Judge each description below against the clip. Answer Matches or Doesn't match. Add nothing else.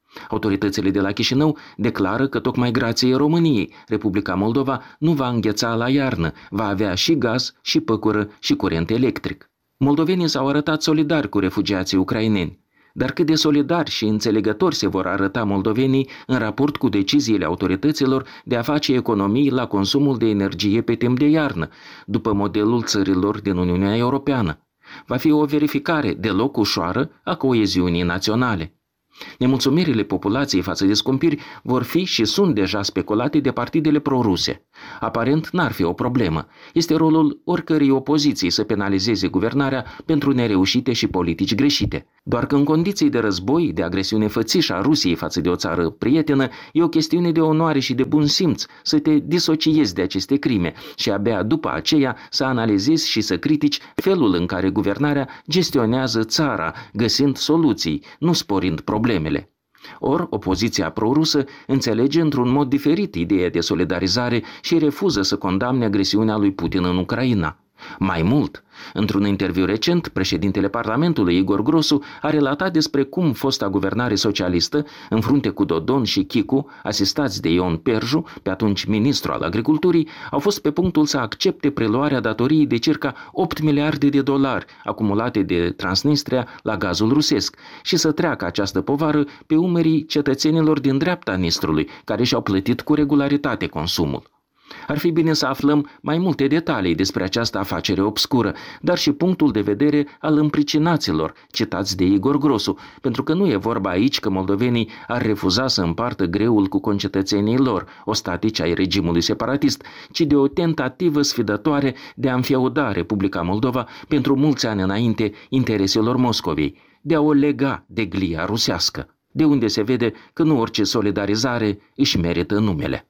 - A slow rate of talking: Doesn't match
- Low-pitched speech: Matches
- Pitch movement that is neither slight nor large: Doesn't match